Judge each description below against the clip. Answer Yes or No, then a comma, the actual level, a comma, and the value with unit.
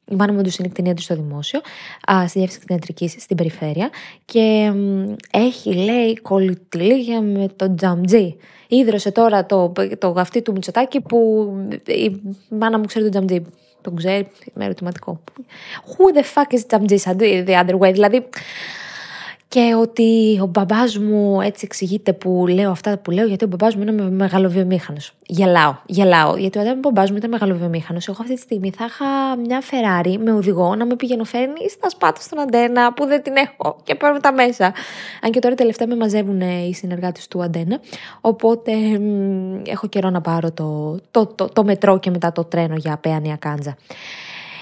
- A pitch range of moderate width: Yes, average, 4.0 semitones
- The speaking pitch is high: Yes, high, 200 Hz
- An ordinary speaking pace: No, fast, 175 wpm